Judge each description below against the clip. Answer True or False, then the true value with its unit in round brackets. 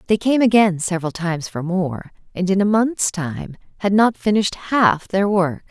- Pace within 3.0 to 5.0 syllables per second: True (4.8 syllables/s)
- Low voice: False (190 Hz)